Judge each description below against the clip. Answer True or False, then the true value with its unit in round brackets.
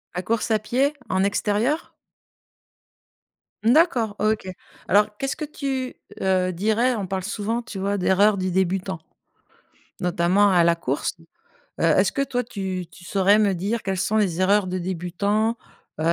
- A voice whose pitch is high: True (200 Hz)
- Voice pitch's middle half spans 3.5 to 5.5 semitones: False (3.1 semitones)